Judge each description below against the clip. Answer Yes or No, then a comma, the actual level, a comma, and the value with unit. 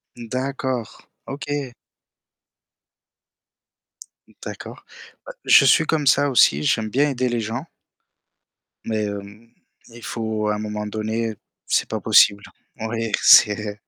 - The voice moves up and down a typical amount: Yes, average, 3.5 semitones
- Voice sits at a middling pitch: No, low, 115 Hz